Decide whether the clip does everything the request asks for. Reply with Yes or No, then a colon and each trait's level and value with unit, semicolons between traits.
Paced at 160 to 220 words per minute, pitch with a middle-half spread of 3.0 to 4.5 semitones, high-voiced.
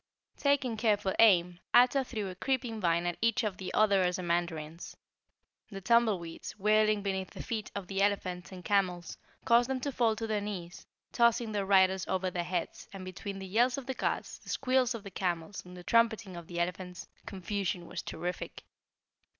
Yes: average, 180 wpm; average, 3.9 semitones; high, 195 Hz